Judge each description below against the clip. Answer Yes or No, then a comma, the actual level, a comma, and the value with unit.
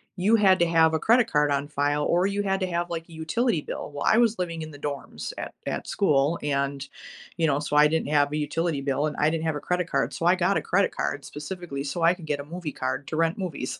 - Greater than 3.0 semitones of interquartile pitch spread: Yes, average, 3.6 semitones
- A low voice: No, medium, 160 Hz